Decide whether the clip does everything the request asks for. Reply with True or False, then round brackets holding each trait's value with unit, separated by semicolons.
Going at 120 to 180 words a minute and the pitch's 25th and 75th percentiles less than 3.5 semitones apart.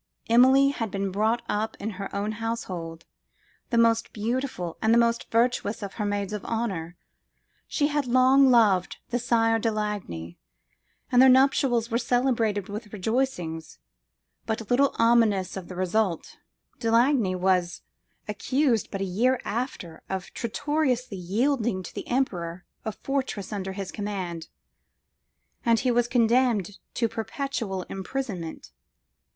False (140 wpm; 4.2 semitones)